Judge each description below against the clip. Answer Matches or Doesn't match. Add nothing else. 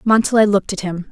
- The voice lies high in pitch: Matches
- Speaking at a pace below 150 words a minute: Doesn't match